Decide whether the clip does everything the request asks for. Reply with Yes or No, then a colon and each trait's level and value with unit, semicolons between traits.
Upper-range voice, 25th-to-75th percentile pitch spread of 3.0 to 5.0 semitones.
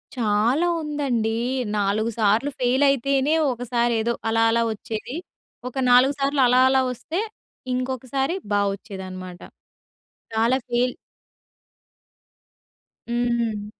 Yes: high, 240 Hz; average, 3.3 semitones